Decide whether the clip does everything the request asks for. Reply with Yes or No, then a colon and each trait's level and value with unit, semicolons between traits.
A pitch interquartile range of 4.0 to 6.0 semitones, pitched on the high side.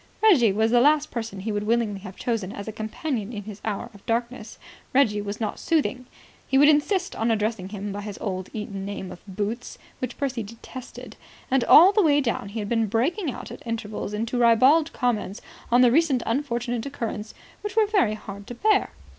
Yes: average, 4.3 semitones; high, 230 Hz